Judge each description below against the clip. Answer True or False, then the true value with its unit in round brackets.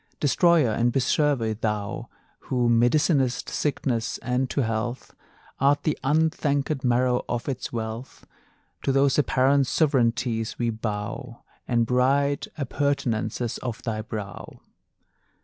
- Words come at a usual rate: False (115 wpm)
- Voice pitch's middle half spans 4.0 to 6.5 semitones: False (3.4 semitones)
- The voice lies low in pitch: True (125 Hz)